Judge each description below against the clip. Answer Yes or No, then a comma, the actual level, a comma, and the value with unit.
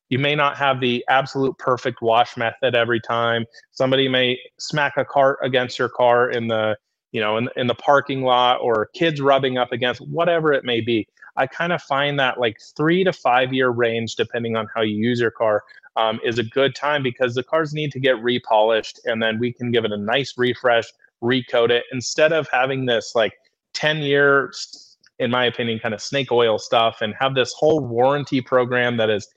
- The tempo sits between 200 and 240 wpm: Yes, fast, 205 wpm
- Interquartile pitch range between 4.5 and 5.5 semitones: No, average, 2.7 semitones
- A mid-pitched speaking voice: No, low, 125 Hz